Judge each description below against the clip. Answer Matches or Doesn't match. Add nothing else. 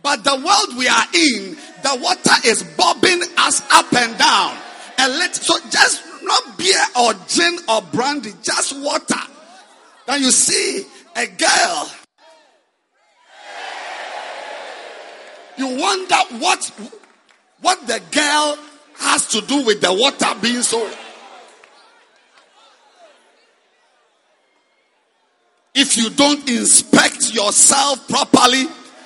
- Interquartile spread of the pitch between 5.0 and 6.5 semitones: Matches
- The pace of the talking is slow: Matches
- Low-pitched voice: Doesn't match